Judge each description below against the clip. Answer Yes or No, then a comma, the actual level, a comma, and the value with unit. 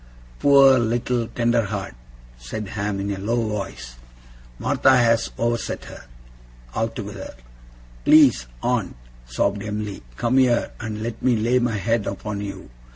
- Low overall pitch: Yes, low, 110 Hz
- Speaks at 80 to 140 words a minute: Yes, slow, 135 wpm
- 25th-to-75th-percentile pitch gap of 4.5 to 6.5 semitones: No, average, 2.8 semitones